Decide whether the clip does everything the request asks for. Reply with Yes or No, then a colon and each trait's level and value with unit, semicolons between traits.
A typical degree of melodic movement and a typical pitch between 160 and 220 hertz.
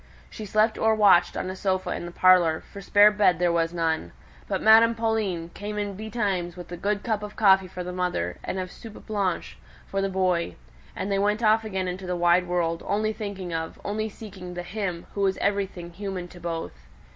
Yes: average, 3.0 semitones; high, 190 Hz